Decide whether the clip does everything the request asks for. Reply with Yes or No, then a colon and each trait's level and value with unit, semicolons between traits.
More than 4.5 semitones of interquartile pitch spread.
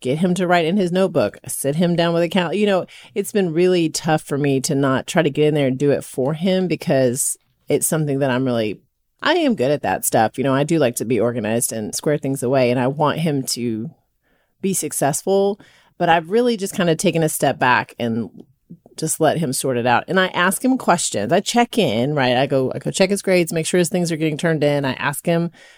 Yes: average, 5.1 semitones